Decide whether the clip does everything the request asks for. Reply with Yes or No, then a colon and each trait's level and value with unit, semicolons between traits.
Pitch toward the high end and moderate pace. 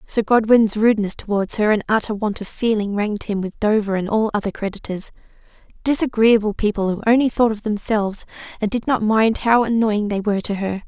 Yes: high, 215 Hz; average, 190 wpm